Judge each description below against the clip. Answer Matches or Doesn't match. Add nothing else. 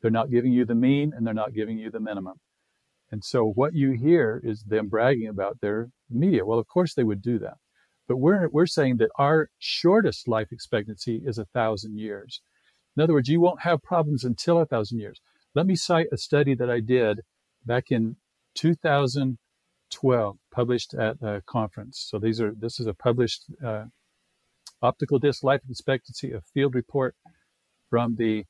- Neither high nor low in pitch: Doesn't match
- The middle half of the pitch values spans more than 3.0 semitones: Matches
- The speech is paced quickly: Doesn't match